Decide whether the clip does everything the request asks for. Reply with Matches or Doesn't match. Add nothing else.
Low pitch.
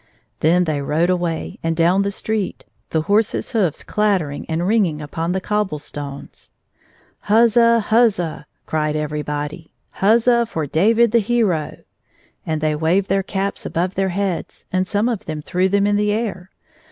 Doesn't match